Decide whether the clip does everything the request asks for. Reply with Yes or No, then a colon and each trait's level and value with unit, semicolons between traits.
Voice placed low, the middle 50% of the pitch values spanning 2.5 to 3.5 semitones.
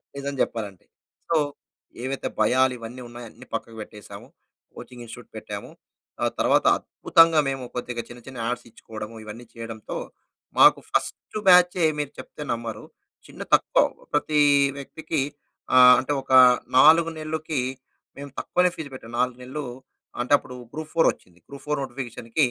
No: low, 130 Hz; average, 4.3 semitones